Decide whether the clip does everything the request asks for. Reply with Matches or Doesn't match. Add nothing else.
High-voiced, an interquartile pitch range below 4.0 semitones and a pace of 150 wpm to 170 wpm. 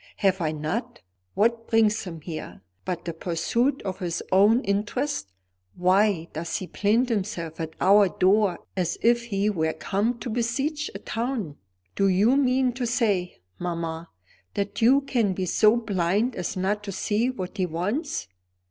Doesn't match